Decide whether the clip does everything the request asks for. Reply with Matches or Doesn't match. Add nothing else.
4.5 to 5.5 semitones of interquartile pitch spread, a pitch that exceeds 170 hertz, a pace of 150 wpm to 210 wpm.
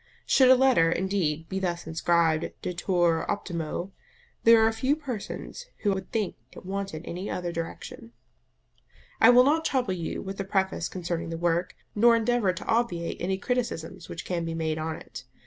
Matches